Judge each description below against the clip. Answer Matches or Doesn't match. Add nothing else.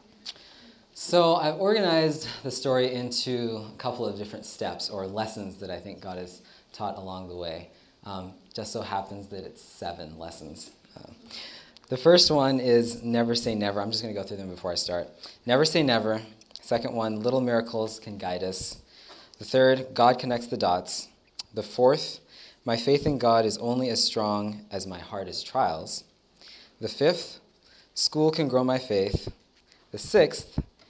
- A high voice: Doesn't match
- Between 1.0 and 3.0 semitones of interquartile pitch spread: Doesn't match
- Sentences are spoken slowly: Doesn't match